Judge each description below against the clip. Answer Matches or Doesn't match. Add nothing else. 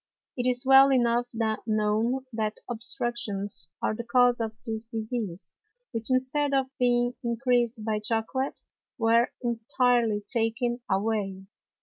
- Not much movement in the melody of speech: Matches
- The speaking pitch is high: Matches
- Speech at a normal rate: Doesn't match